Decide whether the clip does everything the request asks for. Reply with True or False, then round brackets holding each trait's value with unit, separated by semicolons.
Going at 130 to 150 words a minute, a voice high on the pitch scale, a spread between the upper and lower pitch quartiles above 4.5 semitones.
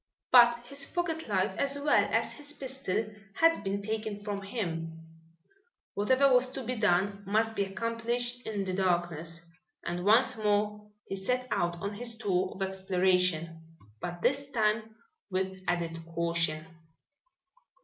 True (140 wpm; 205 Hz; 4.9 semitones)